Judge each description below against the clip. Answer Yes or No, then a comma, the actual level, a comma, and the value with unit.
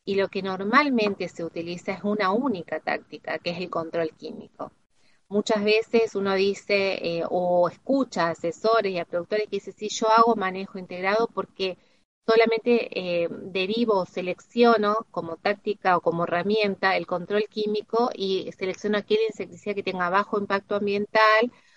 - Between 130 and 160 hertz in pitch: No, high, 200 Hz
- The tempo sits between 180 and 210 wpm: No, average, 155 wpm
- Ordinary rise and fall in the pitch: Yes, average, 3.3 semitones